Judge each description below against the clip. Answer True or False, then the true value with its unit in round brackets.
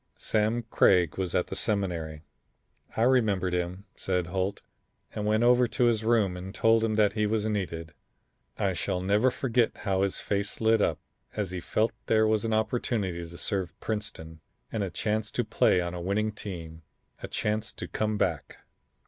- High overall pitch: False (100 Hz)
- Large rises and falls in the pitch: False (3.3 semitones)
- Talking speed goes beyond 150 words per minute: True (180 wpm)